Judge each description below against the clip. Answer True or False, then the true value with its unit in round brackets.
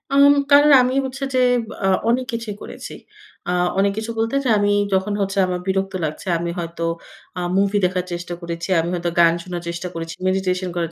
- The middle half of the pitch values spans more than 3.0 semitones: True (4.1 semitones)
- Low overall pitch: False (190 Hz)